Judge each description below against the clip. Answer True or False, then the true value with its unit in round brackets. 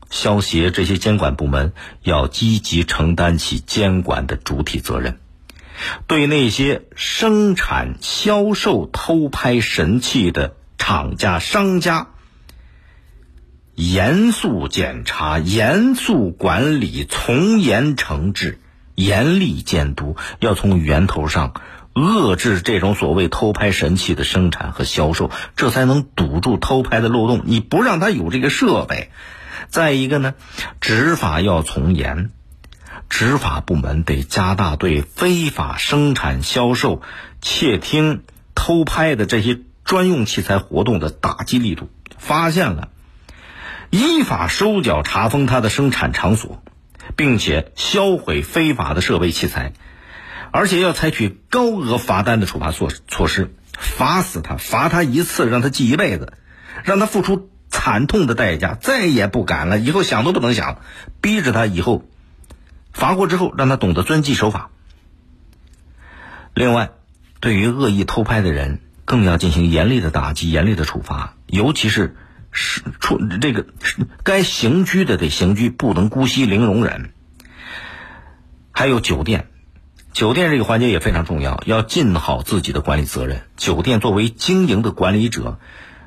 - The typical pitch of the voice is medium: False (95 Hz)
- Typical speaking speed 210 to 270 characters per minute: True (215 characters per minute)